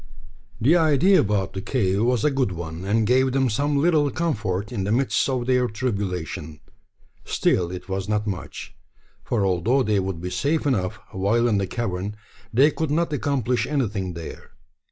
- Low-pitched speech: Yes, low, 110 Hz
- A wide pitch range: Yes, wide, 6.0 semitones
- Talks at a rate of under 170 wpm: No, average, 175 wpm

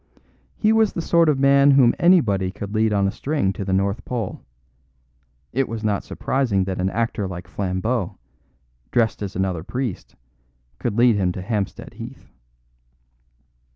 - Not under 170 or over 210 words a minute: No, average, 155 wpm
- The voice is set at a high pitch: No, low, 110 Hz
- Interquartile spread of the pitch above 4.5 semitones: Yes, wide, 5.5 semitones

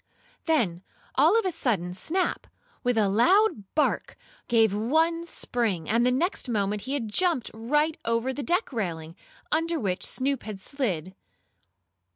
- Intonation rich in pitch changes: Yes, wide, 7.4 semitones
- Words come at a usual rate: Yes, average, 150 wpm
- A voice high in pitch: Yes, high, 245 Hz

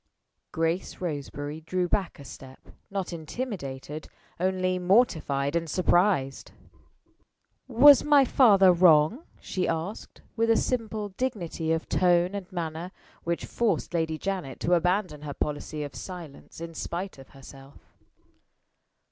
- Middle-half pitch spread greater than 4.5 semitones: No, average, 4.1 semitones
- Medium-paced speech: No, slow, 125 wpm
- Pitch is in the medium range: Yes, medium, 175 Hz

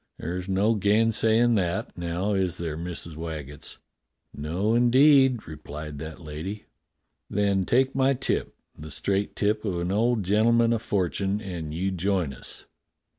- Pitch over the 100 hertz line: No, very low, 95 Hz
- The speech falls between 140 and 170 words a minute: Yes, average, 150 wpm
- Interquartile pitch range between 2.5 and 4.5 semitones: No, average, 4.9 semitones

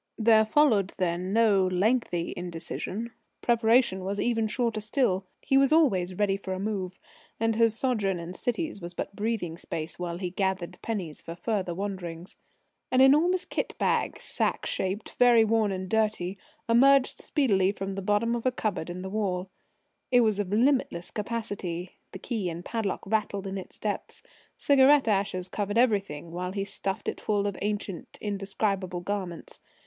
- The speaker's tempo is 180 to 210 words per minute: No, average, 165 wpm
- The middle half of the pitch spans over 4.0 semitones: No, average, 3.6 semitones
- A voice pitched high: Yes, high, 200 Hz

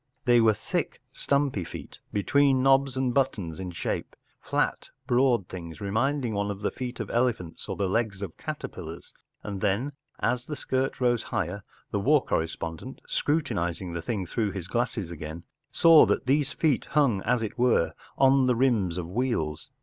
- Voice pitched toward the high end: No, low, 115 Hz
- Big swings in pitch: Yes, wide, 6.1 semitones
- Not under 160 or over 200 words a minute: Yes, average, 170 wpm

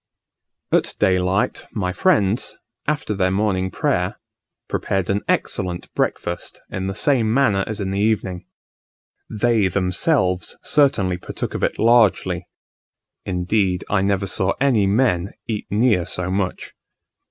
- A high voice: No, low, 100 Hz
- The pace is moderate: No, slow, 130 wpm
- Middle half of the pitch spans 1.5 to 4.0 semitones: Yes, average, 3.0 semitones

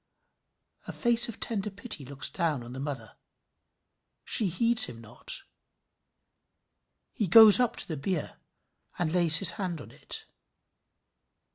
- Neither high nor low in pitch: Yes, medium, 175 Hz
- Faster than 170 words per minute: No, slow, 135 wpm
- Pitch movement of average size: No, wide, 6.9 semitones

